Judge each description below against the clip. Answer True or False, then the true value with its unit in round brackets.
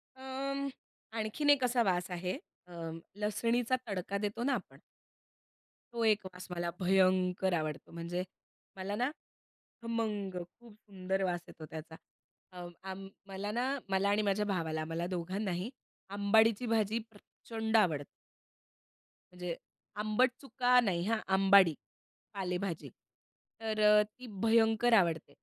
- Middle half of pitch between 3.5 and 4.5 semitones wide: True (3.8 semitones)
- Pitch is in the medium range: False (200 Hz)